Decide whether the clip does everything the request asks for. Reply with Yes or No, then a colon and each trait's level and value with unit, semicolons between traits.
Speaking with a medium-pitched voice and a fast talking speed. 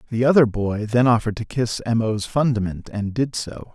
No: low, 115 Hz; fast, 210 wpm